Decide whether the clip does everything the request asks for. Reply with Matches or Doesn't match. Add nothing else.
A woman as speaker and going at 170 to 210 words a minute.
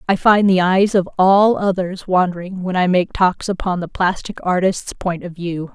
Matches